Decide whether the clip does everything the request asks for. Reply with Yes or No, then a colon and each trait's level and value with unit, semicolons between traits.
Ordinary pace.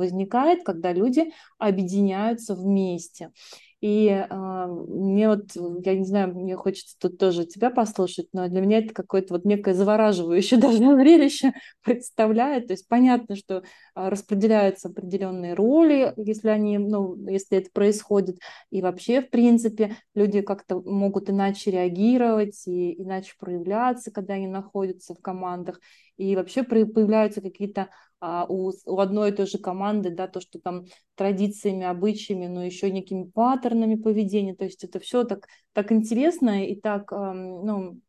Yes: average, 140 wpm